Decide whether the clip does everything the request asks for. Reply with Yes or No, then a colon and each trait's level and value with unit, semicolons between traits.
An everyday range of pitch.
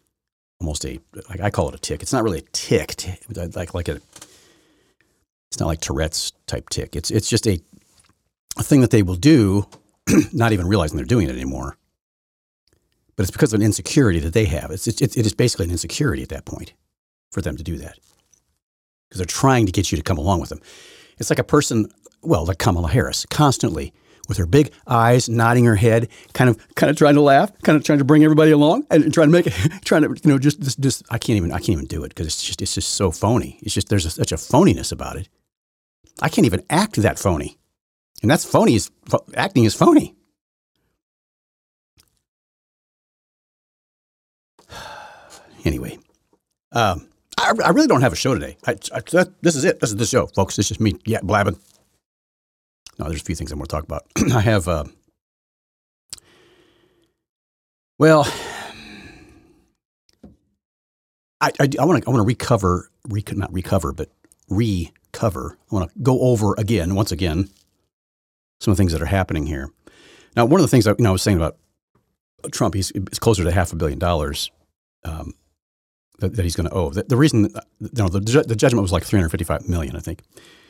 No: wide, 6.2 semitones